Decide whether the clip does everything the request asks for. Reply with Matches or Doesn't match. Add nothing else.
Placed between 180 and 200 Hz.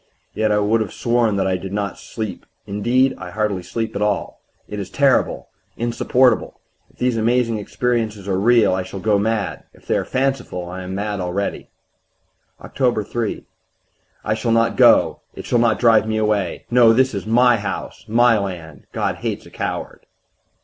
Doesn't match